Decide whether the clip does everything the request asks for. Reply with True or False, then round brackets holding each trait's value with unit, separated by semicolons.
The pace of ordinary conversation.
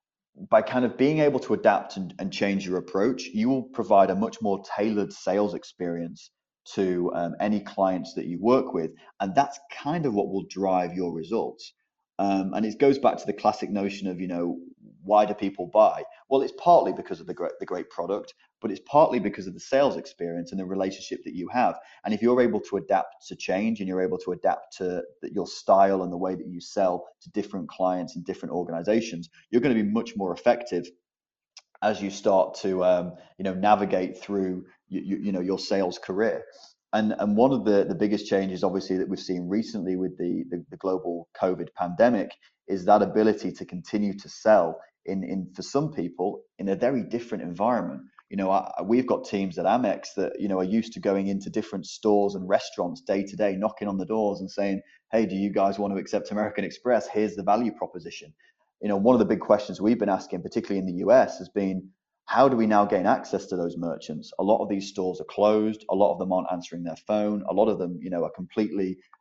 False (225 wpm)